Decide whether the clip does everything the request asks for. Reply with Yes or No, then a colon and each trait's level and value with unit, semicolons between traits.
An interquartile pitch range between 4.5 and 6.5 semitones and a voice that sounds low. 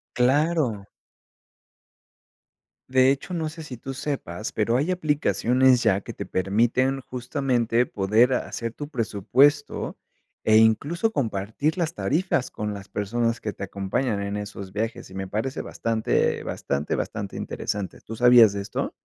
Yes: average, 4.8 semitones; low, 120 Hz